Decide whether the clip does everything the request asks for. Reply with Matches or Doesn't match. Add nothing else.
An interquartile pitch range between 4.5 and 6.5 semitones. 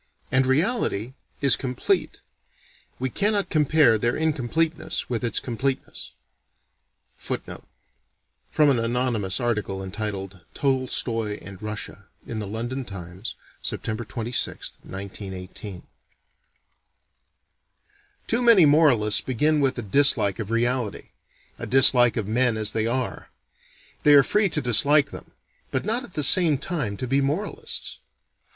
Matches